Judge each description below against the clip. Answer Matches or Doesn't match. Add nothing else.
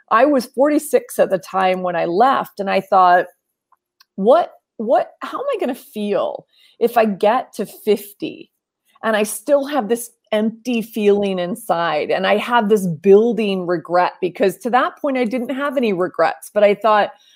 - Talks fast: Doesn't match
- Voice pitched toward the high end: Matches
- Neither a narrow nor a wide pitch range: Doesn't match